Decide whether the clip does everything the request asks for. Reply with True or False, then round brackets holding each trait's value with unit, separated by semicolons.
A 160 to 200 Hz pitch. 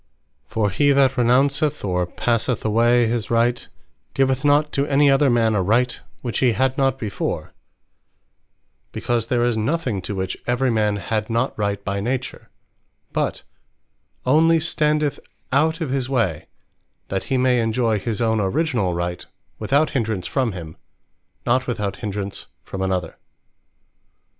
False (120 Hz)